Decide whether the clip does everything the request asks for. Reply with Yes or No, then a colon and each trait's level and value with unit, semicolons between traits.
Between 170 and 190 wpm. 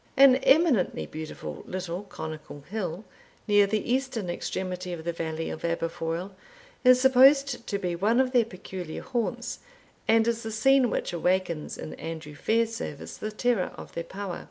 No: average, 155 wpm